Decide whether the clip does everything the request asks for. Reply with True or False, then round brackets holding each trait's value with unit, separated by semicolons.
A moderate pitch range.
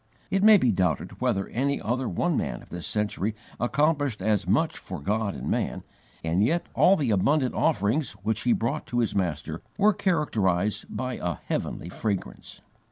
False (6.5 semitones)